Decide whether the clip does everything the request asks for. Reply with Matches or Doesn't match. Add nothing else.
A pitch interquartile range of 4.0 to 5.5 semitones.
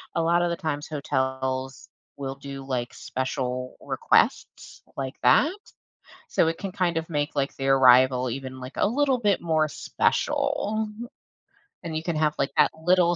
Matches